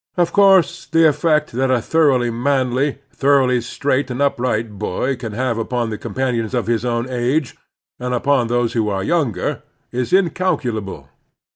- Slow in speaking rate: No, average, 155 wpm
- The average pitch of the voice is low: Yes, low, 125 Hz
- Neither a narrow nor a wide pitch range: Yes, average, 3.4 semitones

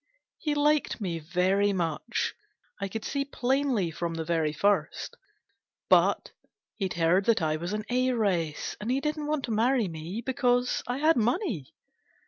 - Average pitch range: No, wide, 7.0 semitones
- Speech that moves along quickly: No, average, 155 wpm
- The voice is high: Yes, high, 210 Hz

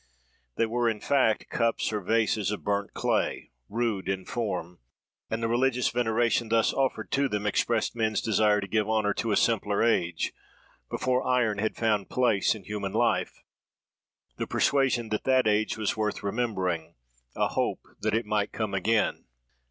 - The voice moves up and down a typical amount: No, narrow, 2.3 semitones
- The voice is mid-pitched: No, low, 110 Hz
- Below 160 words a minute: No, average, 165 wpm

